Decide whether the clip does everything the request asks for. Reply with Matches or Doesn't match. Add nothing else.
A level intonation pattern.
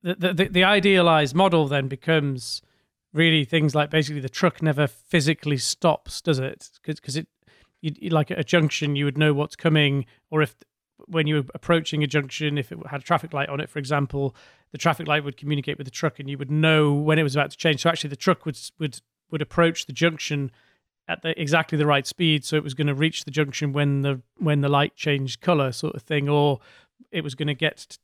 Matches